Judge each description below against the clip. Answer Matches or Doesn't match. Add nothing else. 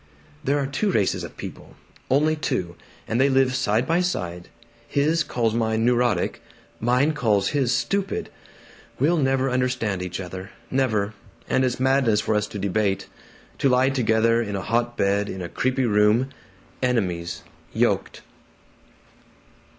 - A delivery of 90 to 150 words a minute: Matches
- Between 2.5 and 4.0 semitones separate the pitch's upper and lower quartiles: Doesn't match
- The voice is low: Matches